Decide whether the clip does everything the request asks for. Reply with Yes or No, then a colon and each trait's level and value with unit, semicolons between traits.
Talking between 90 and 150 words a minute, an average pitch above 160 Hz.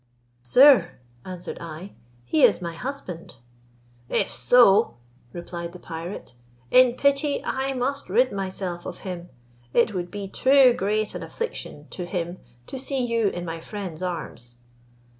Yes: average, 140 wpm; high, 190 Hz